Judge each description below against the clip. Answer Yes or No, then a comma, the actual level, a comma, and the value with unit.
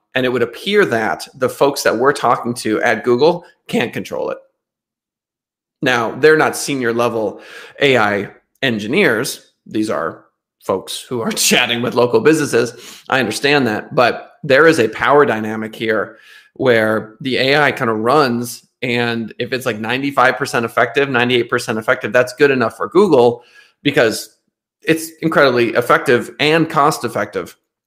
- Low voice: Yes, low, 125 Hz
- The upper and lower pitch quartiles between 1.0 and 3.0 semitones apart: No, average, 3.7 semitones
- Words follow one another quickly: No, average, 145 wpm